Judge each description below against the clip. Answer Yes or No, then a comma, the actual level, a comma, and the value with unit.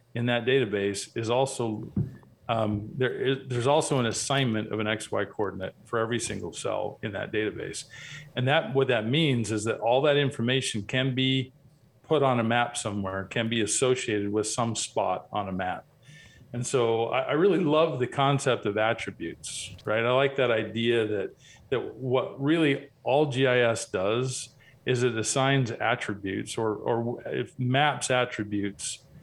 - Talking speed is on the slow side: No, average, 165 wpm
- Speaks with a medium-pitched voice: No, low, 120 Hz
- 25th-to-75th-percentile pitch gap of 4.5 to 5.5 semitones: No, average, 3.5 semitones